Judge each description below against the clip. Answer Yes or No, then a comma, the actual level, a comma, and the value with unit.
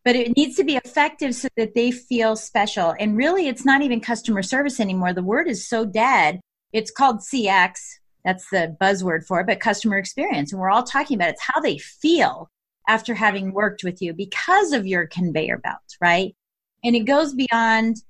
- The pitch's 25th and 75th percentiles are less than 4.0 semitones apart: No, wide, 5.4 semitones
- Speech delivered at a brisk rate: No, average, 195 wpm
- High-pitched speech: Yes, high, 225 Hz